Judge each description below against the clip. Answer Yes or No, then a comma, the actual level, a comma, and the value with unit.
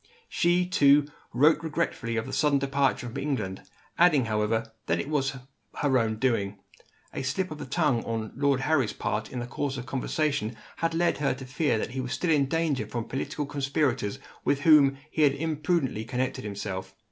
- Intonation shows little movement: No, average, 4.4 semitones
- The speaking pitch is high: No, low, 135 Hz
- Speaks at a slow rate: No, average, 185 wpm